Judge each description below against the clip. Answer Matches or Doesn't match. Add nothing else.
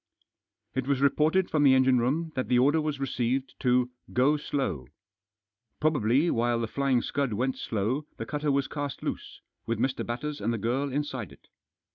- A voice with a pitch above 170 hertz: Doesn't match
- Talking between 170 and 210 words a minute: Matches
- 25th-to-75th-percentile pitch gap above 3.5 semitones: Doesn't match